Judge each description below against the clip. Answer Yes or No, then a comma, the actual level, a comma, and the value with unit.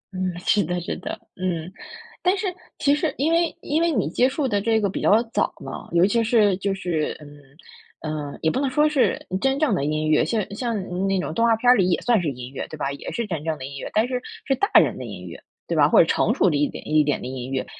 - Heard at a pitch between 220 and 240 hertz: No, high, 195 Hz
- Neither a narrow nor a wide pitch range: No, wide, 8.3 semitones